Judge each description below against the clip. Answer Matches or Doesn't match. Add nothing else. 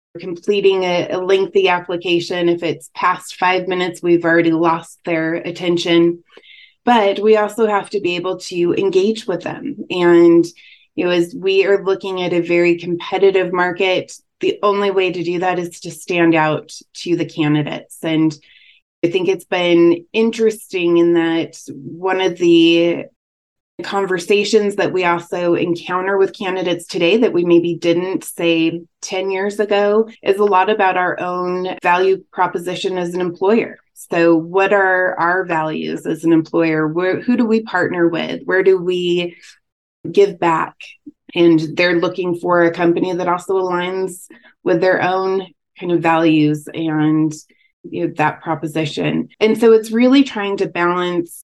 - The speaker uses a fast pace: Doesn't match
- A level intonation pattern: Matches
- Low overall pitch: Doesn't match